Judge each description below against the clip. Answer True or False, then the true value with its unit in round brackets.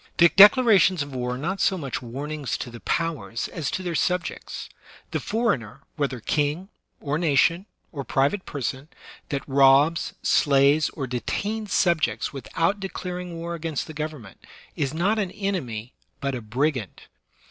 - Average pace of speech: True (150 wpm)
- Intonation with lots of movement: False (4.9 semitones)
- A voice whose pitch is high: False (155 Hz)